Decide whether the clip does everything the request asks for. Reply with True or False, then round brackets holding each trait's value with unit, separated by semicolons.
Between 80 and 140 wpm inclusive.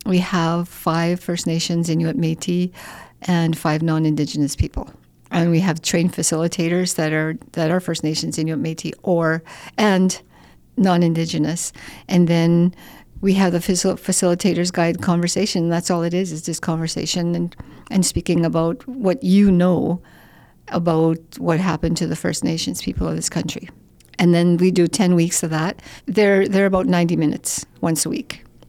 False (160 wpm)